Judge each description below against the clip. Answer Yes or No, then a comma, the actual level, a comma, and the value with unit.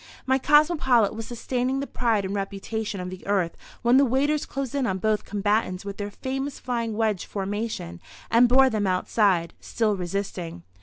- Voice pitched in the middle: No, high, 220 Hz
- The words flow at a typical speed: Yes, average, 170 wpm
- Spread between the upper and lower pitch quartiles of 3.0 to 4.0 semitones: No, average, 4.5 semitones